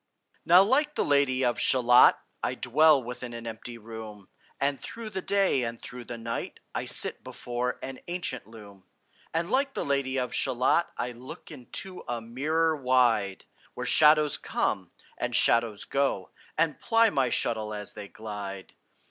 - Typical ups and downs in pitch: Yes, average, 4.8 semitones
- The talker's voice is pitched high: No, low, 125 Hz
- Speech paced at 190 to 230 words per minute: No, average, 160 wpm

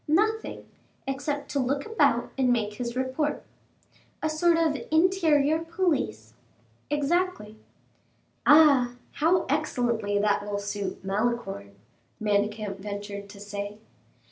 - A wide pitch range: Yes, wide, 7.0 semitones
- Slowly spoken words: Yes, slow, 110 wpm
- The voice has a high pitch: Yes, very high, 250 Hz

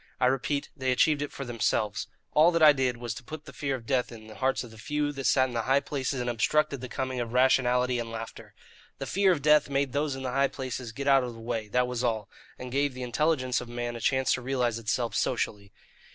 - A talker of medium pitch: No, low, 130 Hz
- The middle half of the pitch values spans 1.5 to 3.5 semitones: Yes, narrow, 2.6 semitones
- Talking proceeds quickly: Yes, fast, 255 wpm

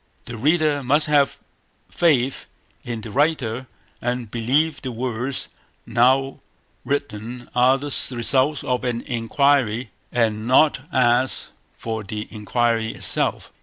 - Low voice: Yes, low, 125 Hz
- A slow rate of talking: Yes, slow, 120 wpm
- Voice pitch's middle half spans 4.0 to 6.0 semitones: No, average, 3.3 semitones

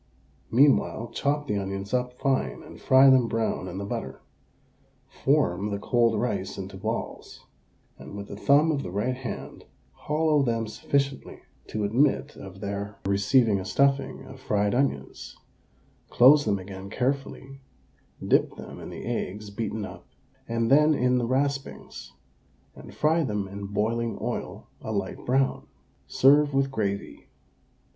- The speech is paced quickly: No, average, 145 wpm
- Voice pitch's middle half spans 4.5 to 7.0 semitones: Yes, average, 5.2 semitones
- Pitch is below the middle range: Yes, low, 115 Hz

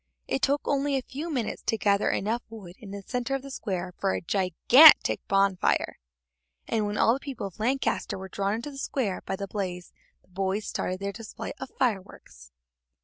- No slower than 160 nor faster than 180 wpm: No, average, 195 wpm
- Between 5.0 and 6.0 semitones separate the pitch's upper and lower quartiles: Yes, average, 5.3 semitones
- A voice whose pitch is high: Yes, high, 210 Hz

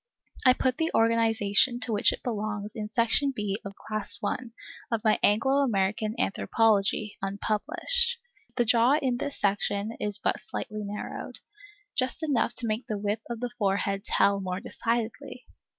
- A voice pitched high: Yes, high, 220 Hz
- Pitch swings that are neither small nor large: Yes, average, 3.0 semitones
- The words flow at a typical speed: Yes, average, 155 wpm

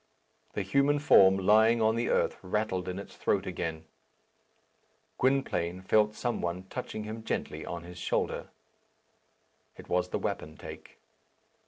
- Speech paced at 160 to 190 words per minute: No, slow, 135 wpm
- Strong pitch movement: No, average, 3.7 semitones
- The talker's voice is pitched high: No, low, 100 Hz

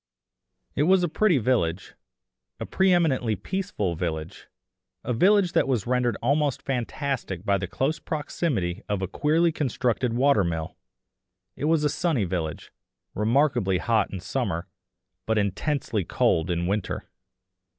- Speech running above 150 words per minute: No, average, 140 wpm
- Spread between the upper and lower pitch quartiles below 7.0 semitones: No, wide, 7.6 semitones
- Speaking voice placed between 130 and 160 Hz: No, low, 120 Hz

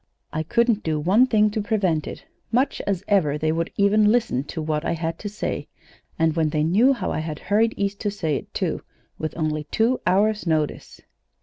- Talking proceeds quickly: Yes, fast, 210 wpm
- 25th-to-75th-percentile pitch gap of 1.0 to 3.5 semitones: No, average, 5.2 semitones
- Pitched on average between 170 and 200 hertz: Yes, medium, 185 Hz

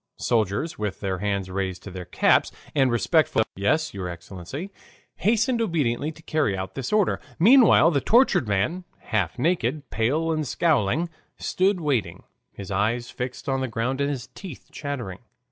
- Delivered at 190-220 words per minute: No, average, 165 wpm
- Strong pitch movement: Yes, wide, 8.3 semitones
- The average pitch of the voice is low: Yes, low, 130 Hz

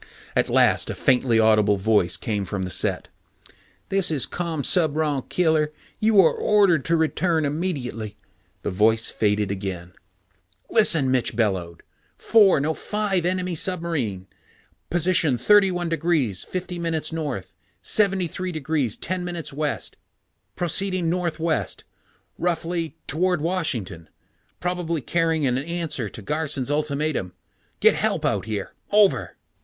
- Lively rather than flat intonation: Yes, wide, 6.8 semitones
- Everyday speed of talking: No, slow, 110 wpm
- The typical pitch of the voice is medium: Yes, medium, 160 Hz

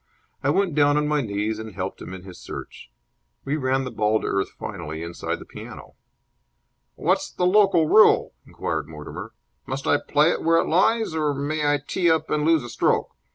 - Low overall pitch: No, medium, 145 Hz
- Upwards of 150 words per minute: Yes, average, 200 wpm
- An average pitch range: No, wide, 7.1 semitones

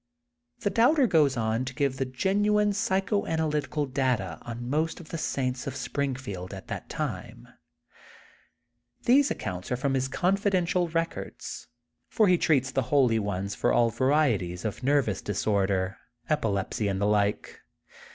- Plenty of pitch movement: Yes, wide, 7.2 semitones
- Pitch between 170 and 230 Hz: No, low, 130 Hz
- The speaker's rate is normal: Yes, average, 150 wpm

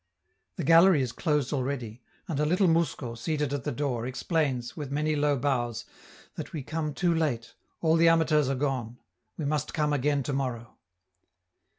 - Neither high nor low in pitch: Yes, medium, 145 Hz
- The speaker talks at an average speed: Yes, average, 170 wpm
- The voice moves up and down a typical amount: Yes, average, 3.6 semitones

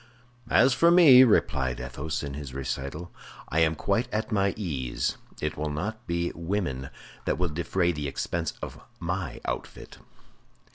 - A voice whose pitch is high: No, very low, 85 Hz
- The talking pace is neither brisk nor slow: Yes, average, 150 wpm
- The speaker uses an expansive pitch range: Yes, wide, 6.7 semitones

